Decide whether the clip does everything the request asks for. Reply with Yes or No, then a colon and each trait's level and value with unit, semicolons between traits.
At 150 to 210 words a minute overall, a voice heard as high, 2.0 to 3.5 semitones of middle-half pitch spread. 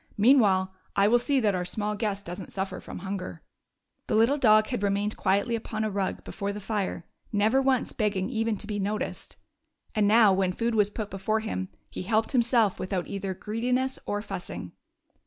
Yes: average, 190 wpm; high, 210 Hz; narrow, 2.5 semitones